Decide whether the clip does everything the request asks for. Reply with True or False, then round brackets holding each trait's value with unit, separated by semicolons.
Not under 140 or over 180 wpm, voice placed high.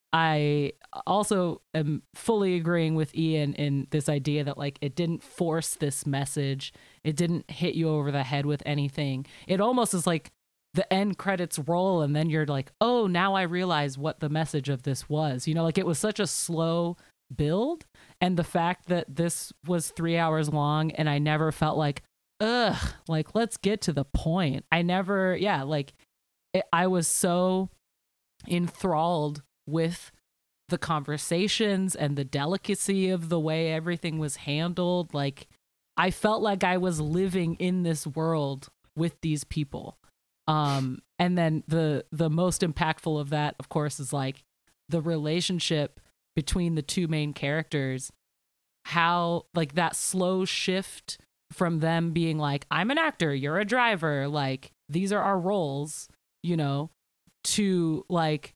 False (160 wpm; 160 Hz)